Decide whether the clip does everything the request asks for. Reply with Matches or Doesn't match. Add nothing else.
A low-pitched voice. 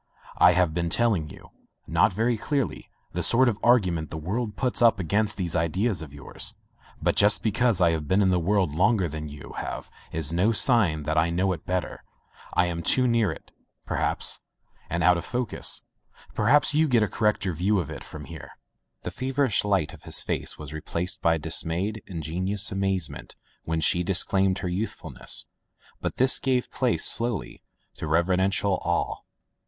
Matches